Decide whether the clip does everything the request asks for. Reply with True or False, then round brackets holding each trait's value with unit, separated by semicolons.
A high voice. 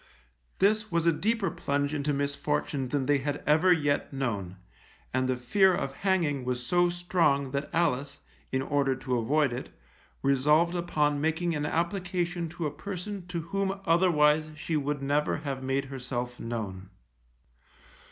False (150 Hz)